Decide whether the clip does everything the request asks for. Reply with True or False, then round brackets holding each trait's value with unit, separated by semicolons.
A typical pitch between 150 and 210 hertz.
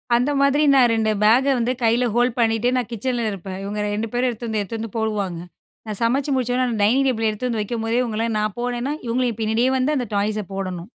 False (230 Hz)